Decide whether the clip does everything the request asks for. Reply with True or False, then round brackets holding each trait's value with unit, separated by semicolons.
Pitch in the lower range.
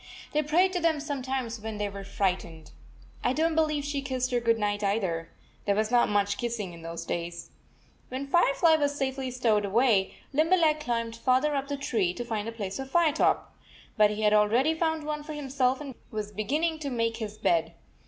False (245 Hz)